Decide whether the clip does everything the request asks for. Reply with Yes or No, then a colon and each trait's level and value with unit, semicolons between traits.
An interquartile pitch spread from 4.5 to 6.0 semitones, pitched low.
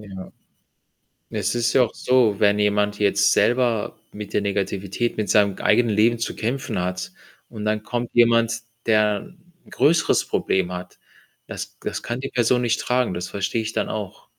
No: average, 2.8 semitones; low, 110 Hz